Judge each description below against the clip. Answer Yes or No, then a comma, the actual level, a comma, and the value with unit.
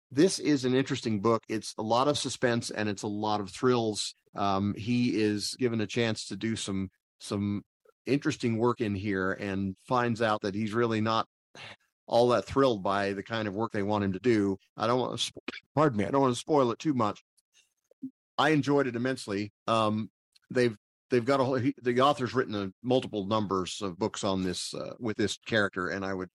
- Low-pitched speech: Yes, low, 110 Hz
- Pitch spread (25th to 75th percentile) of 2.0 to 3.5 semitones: No, average, 3.9 semitones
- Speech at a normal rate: No, fast, 210 wpm